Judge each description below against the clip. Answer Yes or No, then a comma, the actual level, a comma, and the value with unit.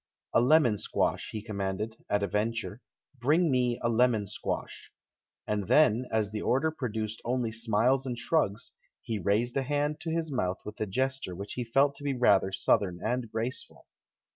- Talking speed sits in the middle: Yes, average, 180 wpm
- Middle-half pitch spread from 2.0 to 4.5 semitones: Yes, average, 4.0 semitones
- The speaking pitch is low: Yes, low, 115 Hz